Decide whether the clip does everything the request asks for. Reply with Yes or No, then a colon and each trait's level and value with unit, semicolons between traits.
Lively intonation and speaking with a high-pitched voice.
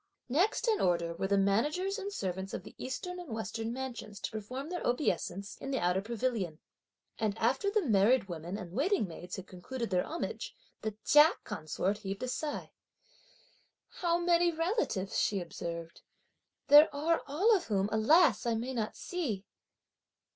Yes: wide, 8.4 semitones; high, 230 Hz